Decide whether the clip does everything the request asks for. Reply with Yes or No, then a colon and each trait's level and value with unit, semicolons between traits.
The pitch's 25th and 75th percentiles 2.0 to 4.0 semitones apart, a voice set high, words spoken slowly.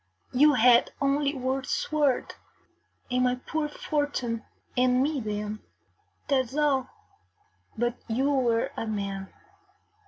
Yes: average, 3.5 semitones; very high, 255 Hz; slow, 120 wpm